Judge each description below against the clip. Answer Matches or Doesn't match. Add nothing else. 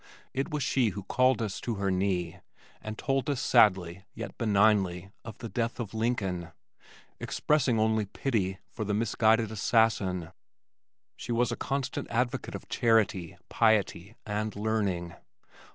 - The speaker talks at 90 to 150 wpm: Matches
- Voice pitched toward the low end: Matches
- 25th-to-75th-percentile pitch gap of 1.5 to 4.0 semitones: Matches